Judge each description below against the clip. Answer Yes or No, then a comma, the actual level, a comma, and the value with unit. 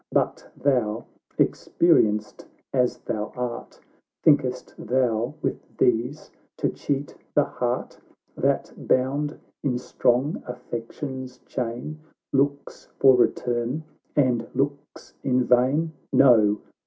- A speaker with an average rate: No, slow, 100 wpm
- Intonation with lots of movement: No, average, 2.8 semitones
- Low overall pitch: Yes, low, 125 Hz